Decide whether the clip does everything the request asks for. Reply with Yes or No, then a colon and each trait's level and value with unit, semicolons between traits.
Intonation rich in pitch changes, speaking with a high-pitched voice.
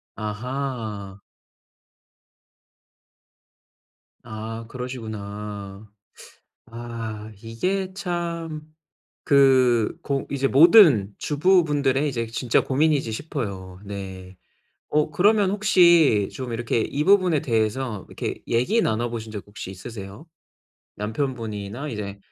No: wide, 5.9 semitones; low, 120 Hz